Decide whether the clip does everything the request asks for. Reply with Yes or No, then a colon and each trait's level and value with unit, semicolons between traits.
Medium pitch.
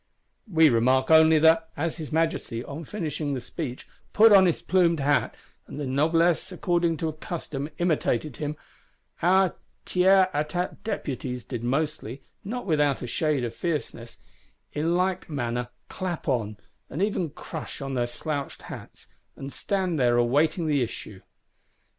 Yes: medium, 155 Hz